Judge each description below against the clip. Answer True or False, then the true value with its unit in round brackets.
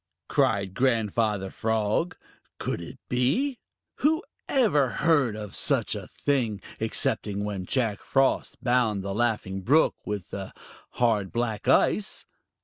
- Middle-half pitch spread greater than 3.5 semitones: True (4.6 semitones)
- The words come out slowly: True (120 wpm)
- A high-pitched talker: False (115 Hz)